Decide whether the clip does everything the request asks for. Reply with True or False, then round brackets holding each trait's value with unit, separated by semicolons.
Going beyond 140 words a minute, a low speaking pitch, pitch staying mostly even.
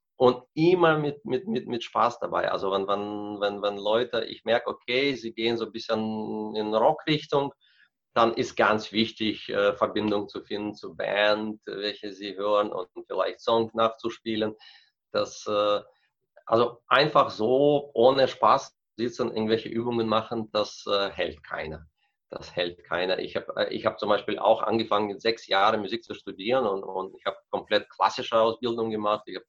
True (160 wpm; 110 Hz; 1.8 semitones)